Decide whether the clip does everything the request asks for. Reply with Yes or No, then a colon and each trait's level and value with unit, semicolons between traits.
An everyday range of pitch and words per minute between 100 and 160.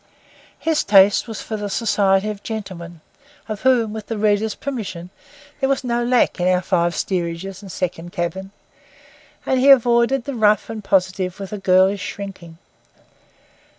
Yes: average, 3.6 semitones; average, 155 wpm